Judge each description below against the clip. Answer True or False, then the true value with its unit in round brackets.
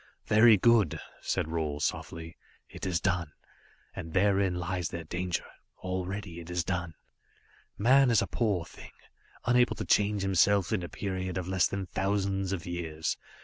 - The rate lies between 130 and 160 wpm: True (155 wpm)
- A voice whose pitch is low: True (95 Hz)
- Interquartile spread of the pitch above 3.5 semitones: False (2.6 semitones)